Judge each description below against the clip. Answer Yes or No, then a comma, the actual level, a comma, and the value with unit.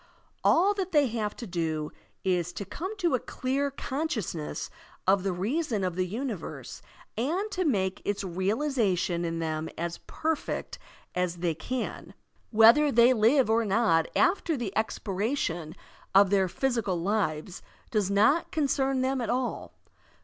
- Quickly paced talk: No, average, 150 wpm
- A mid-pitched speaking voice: No, high, 215 Hz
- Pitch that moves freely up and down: Yes, wide, 6.8 semitones